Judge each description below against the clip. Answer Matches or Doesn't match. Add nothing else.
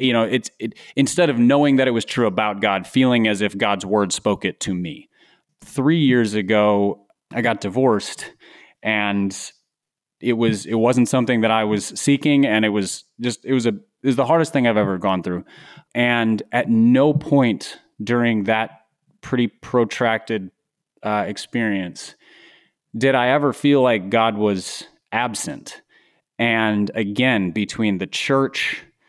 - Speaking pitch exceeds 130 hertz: Doesn't match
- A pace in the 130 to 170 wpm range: Matches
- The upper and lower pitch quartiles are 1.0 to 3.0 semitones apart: Doesn't match